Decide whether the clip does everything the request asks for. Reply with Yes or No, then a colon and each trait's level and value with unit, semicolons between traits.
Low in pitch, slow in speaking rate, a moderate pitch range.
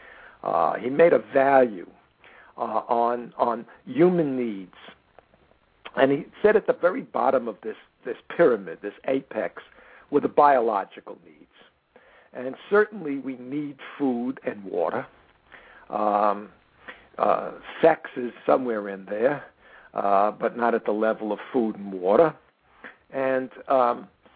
Yes: low, 130 Hz; slow, 130 wpm; average, 4.9 semitones